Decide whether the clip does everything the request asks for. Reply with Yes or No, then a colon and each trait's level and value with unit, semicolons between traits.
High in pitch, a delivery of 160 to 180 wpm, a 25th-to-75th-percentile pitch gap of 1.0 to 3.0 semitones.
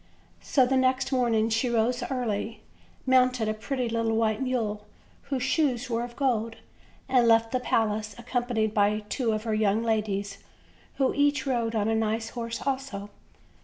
Yes: high, 230 Hz; average, 165 wpm; average, 2.7 semitones